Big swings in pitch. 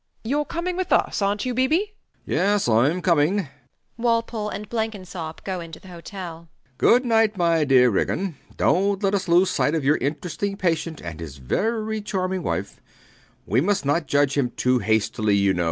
Yes: wide, 6.5 semitones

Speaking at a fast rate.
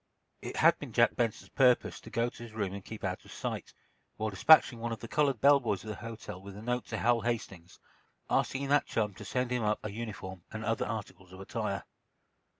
Yes: fast, 225 wpm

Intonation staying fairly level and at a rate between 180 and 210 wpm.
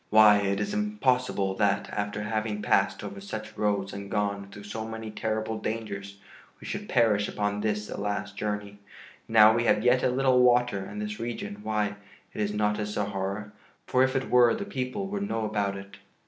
Yes: narrow, 2.0 semitones; average, 190 wpm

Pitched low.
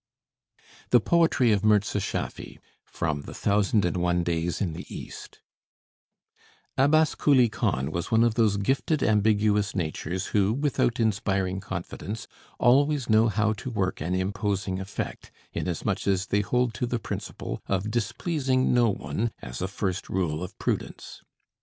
Yes: low, 105 Hz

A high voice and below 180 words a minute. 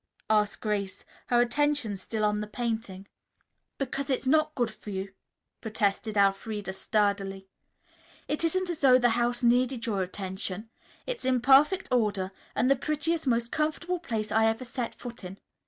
Yes: high, 230 Hz; average, 155 wpm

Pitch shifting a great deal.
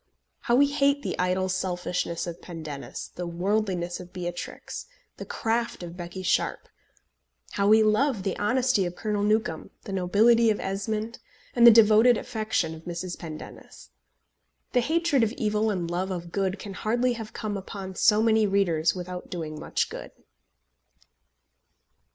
No: average, 3.8 semitones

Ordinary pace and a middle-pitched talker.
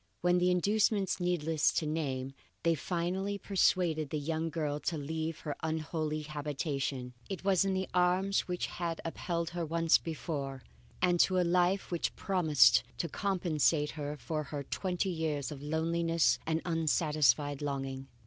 Yes: average, 150 wpm; medium, 160 Hz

